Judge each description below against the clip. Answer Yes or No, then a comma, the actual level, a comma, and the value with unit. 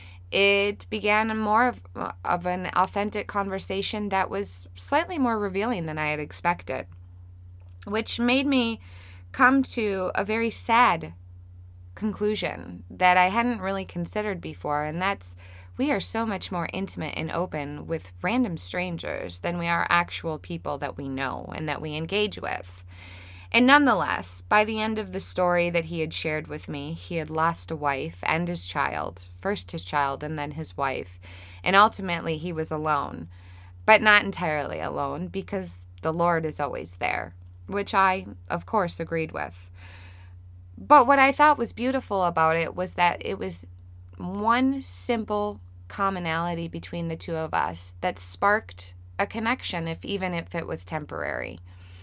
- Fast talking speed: No, average, 160 wpm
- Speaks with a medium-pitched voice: Yes, medium, 165 Hz